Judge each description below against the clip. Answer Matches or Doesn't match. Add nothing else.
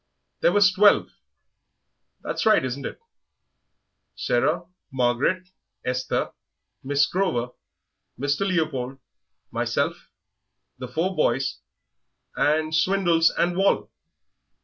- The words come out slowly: Matches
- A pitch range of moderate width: Doesn't match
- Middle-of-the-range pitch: Matches